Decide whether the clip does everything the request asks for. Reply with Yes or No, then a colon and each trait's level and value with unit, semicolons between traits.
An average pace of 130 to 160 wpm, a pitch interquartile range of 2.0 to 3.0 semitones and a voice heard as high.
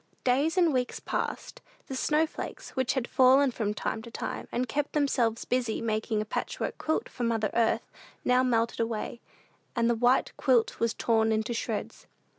No: average, 170 wpm; narrow, 2.6 semitones; high, 240 Hz